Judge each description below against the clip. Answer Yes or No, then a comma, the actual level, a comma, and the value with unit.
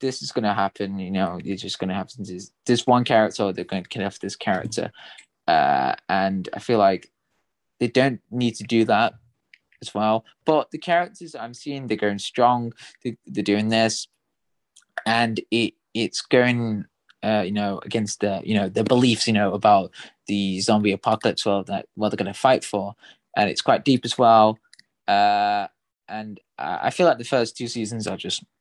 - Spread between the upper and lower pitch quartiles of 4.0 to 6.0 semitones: No, average, 3.0 semitones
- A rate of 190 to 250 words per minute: Yes, average, 195 wpm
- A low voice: Yes, low, 110 Hz